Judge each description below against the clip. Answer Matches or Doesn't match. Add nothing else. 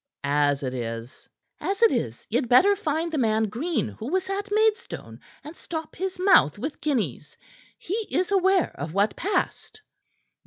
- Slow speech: Doesn't match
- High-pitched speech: Matches